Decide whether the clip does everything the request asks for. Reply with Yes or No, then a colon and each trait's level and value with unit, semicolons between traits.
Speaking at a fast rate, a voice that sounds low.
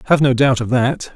Yes: fast, 260 wpm; low, 130 Hz